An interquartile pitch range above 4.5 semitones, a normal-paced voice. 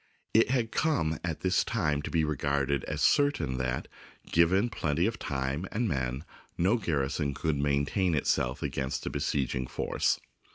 Yes: average, 5.3 semitones; average, 165 wpm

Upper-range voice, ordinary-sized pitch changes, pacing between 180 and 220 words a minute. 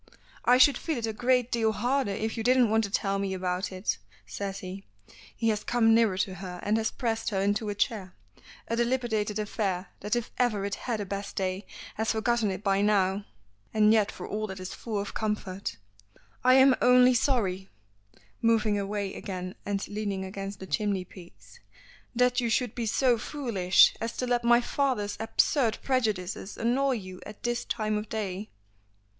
Yes: high, 215 Hz; average, 3.3 semitones; average, 185 wpm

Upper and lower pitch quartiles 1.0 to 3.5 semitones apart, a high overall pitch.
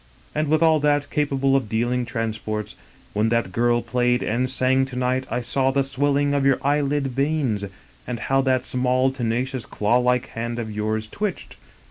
No: average, 2.8 semitones; low, 130 Hz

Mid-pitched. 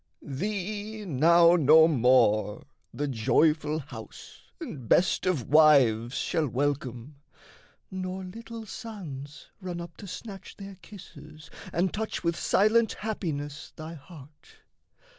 Yes: medium, 160 Hz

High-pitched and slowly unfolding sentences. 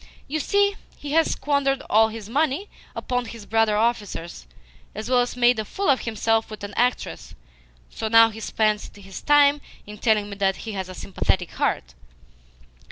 No: high, 225 Hz; average, 175 wpm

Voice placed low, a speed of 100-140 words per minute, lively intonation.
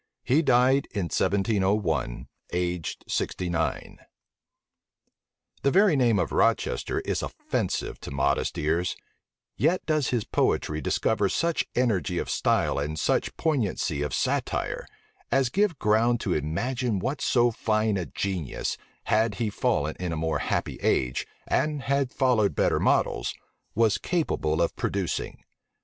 Yes: low, 105 Hz; slow, 135 wpm; wide, 7.2 semitones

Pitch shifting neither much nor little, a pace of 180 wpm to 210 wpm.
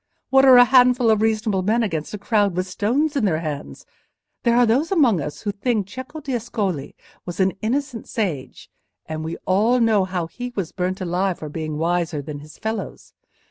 No: wide, 5.8 semitones; average, 185 wpm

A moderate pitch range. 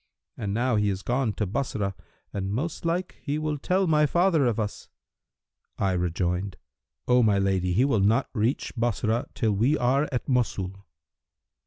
No: wide, 5.8 semitones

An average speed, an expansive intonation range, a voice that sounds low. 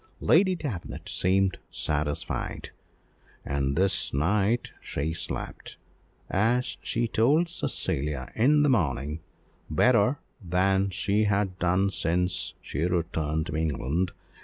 No: slow, 110 wpm; wide, 5.7 semitones; very low, 95 Hz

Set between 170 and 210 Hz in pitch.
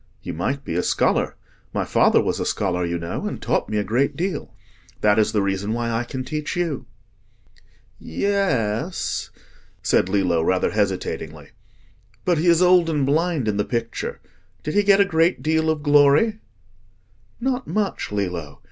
No: low, 135 Hz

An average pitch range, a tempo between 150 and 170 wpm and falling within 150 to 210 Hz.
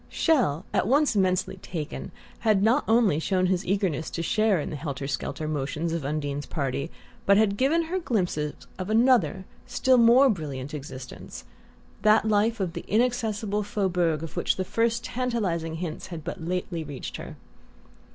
No: wide, 6.1 semitones; average, 160 wpm; medium, 185 Hz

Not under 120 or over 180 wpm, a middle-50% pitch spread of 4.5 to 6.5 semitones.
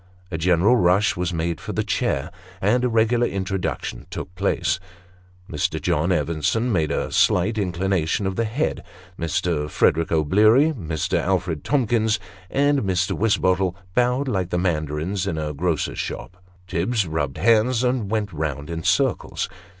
Yes: average, 150 wpm; average, 5.3 semitones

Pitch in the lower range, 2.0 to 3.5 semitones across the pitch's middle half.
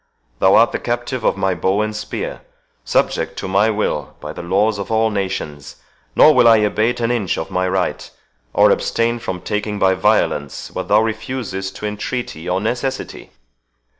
Yes: low, 105 Hz; average, 3.1 semitones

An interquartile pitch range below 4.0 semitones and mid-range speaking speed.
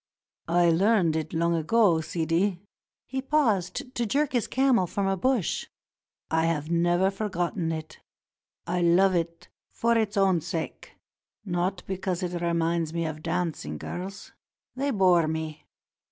Yes: average, 3.2 semitones; average, 145 wpm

